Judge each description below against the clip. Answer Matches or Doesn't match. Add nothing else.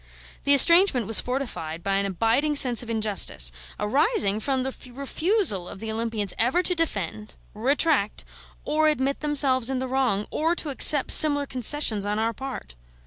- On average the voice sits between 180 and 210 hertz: Doesn't match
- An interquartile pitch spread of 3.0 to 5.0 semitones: Doesn't match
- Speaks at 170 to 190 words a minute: Doesn't match